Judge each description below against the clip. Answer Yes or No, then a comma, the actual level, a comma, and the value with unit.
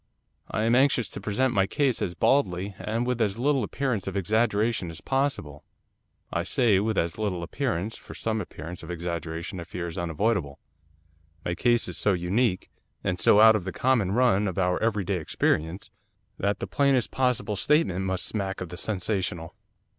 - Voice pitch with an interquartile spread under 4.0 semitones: No, average, 4.7 semitones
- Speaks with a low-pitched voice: Yes, low, 100 Hz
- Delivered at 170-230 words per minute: Yes, average, 180 wpm